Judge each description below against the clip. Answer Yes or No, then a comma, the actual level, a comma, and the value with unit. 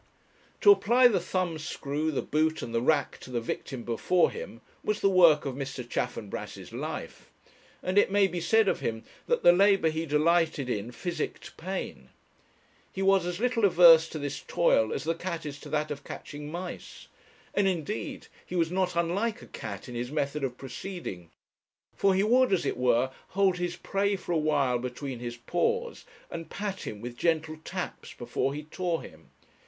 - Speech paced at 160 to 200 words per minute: Yes, average, 185 wpm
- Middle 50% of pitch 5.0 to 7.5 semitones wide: Yes, wide, 5.5 semitones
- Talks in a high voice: No, medium, 165 Hz